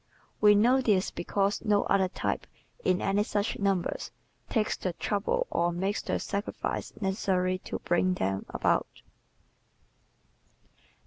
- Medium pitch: No, high, 195 Hz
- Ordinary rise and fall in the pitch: No, narrow, 2.1 semitones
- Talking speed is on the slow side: Yes, slow, 125 wpm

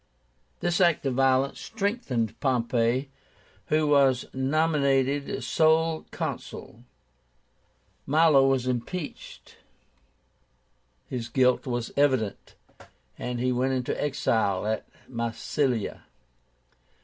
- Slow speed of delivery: Yes, slow, 90 wpm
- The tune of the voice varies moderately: Yes, average, 3.2 semitones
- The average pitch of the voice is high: No, low, 135 Hz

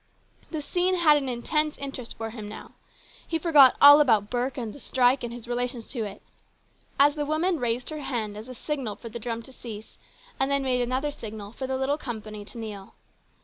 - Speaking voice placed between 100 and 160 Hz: No, very high, 250 Hz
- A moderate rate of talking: No, fast, 215 wpm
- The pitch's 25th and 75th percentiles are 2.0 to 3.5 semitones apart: No, average, 4.1 semitones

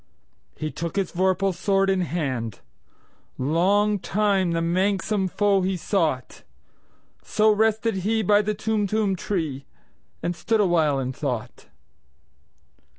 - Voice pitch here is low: No, high, 190 Hz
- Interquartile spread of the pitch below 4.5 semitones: Yes, average, 3.7 semitones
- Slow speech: Yes, slow, 105 wpm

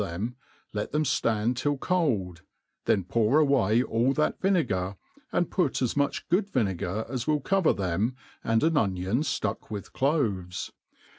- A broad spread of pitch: Yes, wide, 6.8 semitones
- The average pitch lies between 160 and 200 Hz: No, low, 120 Hz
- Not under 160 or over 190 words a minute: No, average, 150 wpm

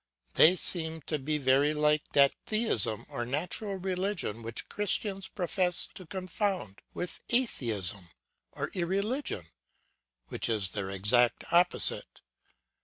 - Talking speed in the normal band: No, slow, 115 wpm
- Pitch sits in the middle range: Yes, medium, 160 Hz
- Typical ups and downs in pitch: No, wide, 8.2 semitones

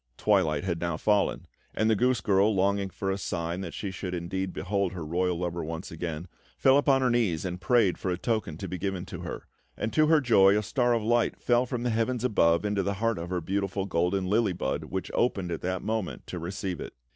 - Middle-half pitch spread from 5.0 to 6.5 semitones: No, average, 4.1 semitones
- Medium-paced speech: No, fast, 230 wpm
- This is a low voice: Yes, very low, 95 Hz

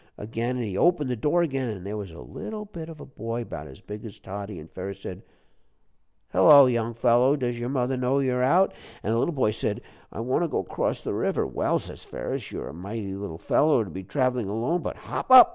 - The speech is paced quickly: Yes, fast, 230 wpm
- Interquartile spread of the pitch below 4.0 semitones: No, average, 5.1 semitones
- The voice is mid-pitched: No, low, 120 Hz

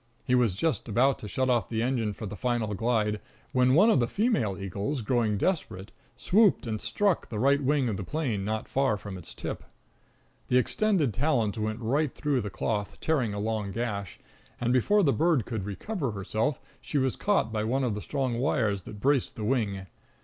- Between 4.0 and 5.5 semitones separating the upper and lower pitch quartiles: Yes, average, 4.7 semitones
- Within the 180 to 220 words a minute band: Yes, average, 200 wpm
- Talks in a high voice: No, low, 120 Hz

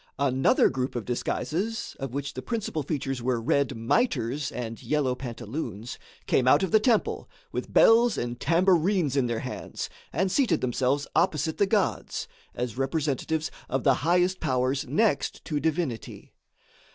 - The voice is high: No, medium, 140 Hz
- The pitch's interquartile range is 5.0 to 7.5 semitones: Yes, wide, 5.5 semitones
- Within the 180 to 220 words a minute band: No, average, 150 wpm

